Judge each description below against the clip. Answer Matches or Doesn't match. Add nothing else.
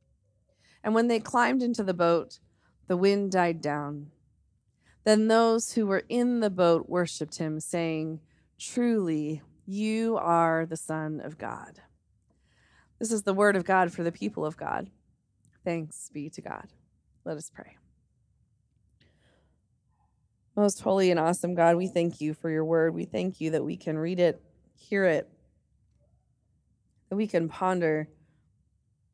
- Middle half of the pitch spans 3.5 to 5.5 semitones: Matches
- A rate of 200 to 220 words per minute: Doesn't match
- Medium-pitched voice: Matches